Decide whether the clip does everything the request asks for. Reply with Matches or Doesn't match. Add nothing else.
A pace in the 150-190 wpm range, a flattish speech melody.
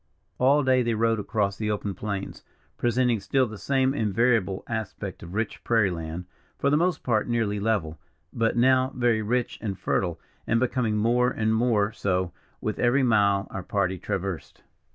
Doesn't match